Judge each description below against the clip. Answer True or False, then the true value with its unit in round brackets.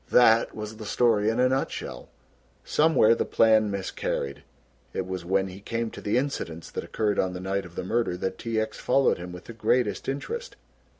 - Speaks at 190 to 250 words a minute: True (195 wpm)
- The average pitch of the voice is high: False (110 Hz)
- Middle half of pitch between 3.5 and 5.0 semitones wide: True (3.9 semitones)